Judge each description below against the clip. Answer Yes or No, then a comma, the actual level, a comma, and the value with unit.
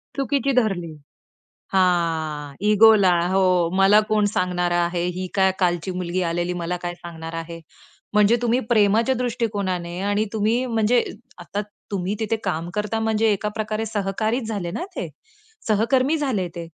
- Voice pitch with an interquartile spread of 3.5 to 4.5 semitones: Yes, average, 4.1 semitones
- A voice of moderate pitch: No, high, 200 Hz